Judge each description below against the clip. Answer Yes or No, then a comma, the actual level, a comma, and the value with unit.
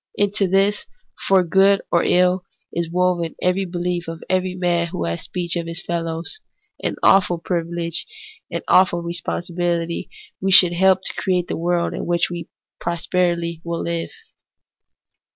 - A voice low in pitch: No, medium, 175 Hz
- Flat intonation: Yes, narrow, 1.3 semitones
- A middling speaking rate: Yes, average, 150 wpm